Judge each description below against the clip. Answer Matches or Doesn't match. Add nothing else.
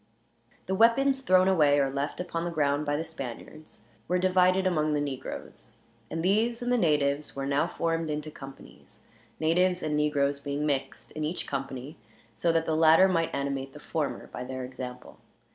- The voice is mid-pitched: Matches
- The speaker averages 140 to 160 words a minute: Doesn't match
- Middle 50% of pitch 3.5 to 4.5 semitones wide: Matches